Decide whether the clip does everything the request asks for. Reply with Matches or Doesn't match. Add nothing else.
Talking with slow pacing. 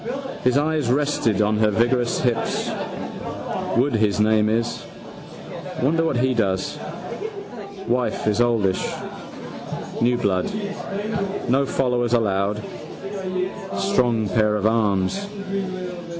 Matches